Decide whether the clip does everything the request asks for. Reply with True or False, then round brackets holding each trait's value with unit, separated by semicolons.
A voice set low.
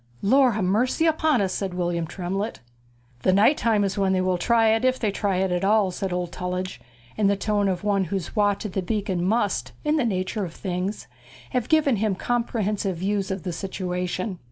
False (195 Hz)